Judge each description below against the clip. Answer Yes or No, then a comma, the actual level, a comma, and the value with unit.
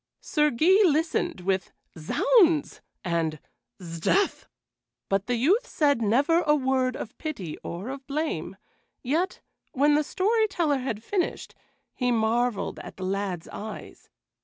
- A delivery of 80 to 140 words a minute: Yes, slow, 135 wpm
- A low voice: No, very high, 260 Hz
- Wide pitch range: Yes, wide, 7.9 semitones